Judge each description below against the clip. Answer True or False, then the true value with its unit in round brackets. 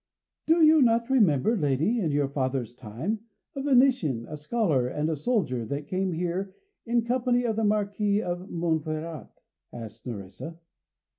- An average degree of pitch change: False (8.3 semitones)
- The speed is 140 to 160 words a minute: True (150 wpm)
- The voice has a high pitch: False (175 Hz)